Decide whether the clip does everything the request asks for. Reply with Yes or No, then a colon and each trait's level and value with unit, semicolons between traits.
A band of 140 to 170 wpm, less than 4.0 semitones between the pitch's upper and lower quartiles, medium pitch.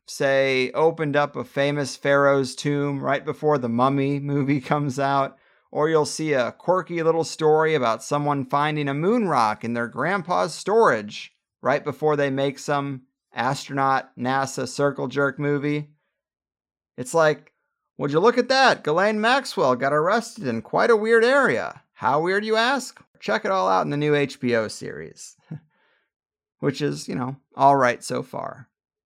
Yes: average, 160 wpm; average, 2.8 semitones; medium, 145 Hz